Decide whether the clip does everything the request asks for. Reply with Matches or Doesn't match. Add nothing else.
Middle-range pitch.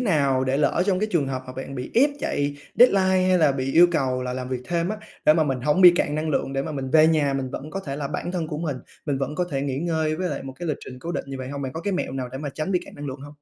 Matches